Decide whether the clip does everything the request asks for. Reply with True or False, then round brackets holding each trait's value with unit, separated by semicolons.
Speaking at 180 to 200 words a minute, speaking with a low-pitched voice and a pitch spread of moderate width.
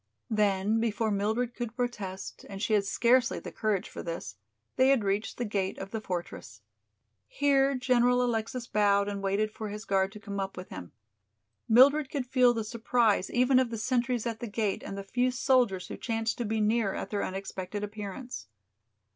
False (190 wpm; 220 Hz; 3.7 semitones)